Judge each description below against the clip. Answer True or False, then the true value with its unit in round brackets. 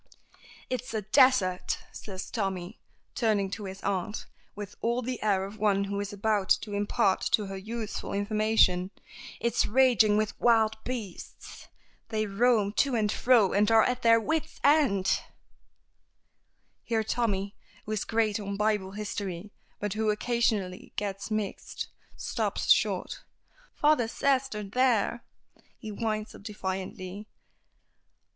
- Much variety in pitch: False (2.5 semitones)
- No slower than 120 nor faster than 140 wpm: True (135 wpm)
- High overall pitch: True (215 Hz)